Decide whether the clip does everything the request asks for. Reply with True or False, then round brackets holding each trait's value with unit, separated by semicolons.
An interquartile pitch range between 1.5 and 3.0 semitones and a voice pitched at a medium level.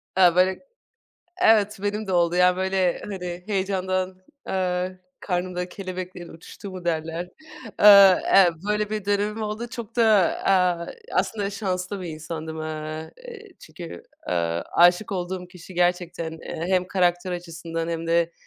True (2.4 semitones; 180 Hz)